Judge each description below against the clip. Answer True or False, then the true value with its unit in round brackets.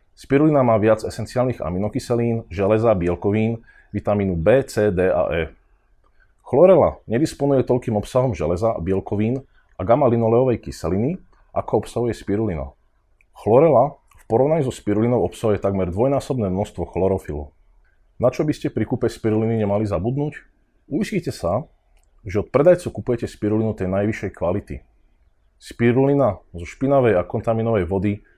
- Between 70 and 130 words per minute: True (125 wpm)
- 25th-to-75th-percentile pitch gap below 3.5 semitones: False (4.2 semitones)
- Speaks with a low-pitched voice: True (110 Hz)